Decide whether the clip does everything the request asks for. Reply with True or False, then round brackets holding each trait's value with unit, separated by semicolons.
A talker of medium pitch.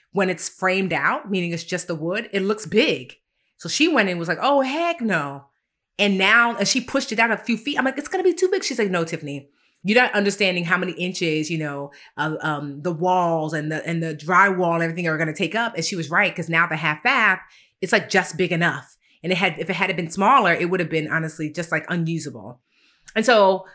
True (180 Hz)